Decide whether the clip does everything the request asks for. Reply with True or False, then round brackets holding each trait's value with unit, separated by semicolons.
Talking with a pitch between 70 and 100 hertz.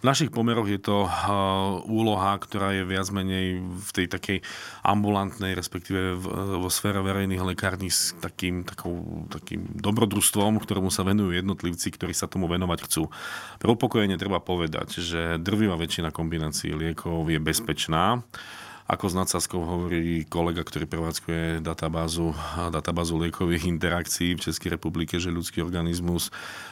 True (90 Hz)